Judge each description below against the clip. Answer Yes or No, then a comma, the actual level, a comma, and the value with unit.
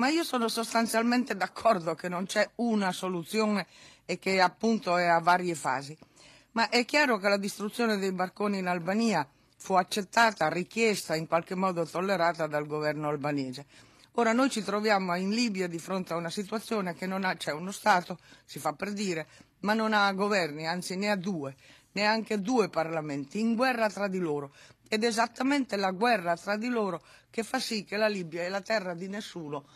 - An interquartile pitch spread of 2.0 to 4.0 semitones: No, average, 4.7 semitones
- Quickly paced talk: Yes, fast, 190 wpm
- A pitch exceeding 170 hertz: Yes, high, 190 Hz